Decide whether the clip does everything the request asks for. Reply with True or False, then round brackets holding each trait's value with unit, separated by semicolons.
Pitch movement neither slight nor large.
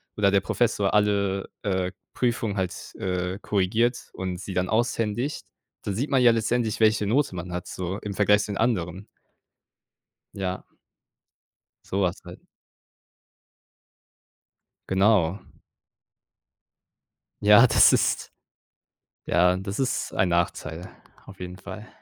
True (3.1 semitones)